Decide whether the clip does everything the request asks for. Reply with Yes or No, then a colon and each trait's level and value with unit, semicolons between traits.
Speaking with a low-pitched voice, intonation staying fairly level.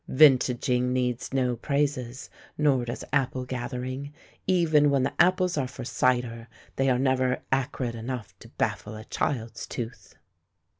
Yes: low, 130 Hz; narrow, 2.2 semitones